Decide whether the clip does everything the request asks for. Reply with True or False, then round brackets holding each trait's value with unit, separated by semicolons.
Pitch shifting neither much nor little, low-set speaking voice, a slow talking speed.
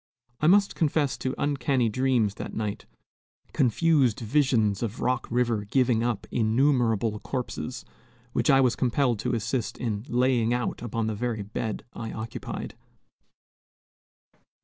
True (3.0 semitones; 120 Hz; 130 wpm)